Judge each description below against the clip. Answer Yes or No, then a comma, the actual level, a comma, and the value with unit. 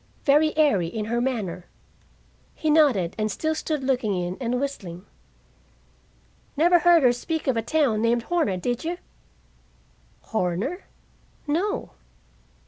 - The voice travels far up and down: Yes, wide, 6.8 semitones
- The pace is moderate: No, slow, 130 wpm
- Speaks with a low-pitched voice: No, very high, 250 Hz